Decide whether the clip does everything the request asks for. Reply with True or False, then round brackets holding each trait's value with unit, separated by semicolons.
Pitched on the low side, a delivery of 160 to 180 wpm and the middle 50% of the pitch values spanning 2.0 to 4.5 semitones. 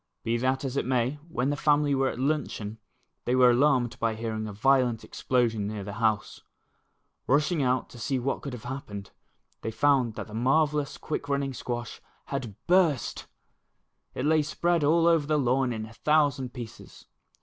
True (130 Hz; 175 wpm; 3.9 semitones)